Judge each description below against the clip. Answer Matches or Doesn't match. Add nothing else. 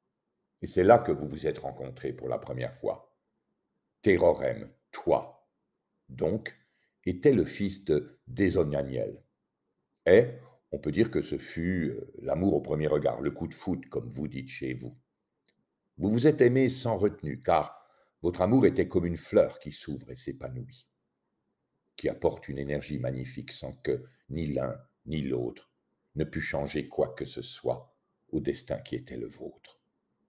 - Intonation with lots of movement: Matches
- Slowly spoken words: Doesn't match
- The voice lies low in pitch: Matches